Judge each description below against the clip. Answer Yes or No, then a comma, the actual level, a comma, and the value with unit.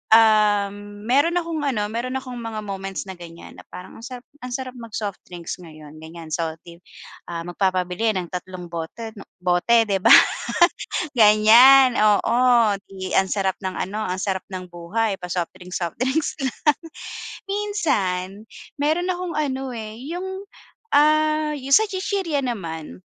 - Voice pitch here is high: Yes, high, 215 Hz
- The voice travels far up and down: Yes, wide, 6.4 semitones